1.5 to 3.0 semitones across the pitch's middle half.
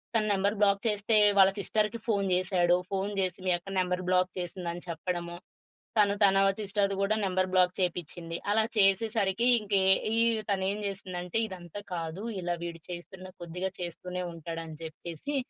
Yes: narrow, 2.4 semitones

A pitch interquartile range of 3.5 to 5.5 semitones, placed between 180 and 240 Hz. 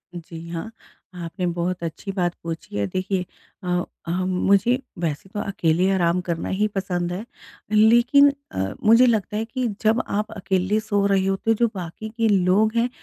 Yes: average, 3.8 semitones; high, 190 Hz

